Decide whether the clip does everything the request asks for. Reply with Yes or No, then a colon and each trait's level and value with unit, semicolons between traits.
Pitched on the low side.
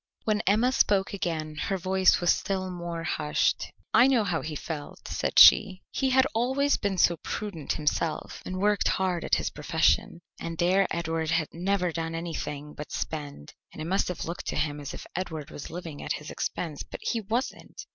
No: medium, 175 Hz